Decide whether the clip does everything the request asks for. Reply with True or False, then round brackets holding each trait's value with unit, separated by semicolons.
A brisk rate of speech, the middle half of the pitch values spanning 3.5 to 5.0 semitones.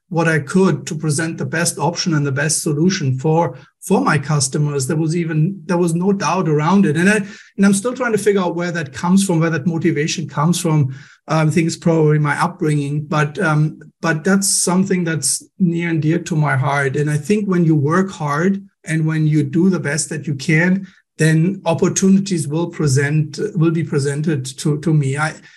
False (210 wpm; 2.7 semitones)